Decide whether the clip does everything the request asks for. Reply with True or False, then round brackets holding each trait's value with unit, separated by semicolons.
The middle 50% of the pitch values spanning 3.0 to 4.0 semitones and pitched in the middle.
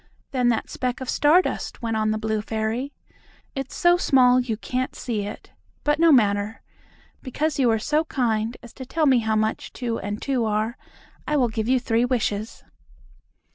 False (3.4 semitones; 240 Hz)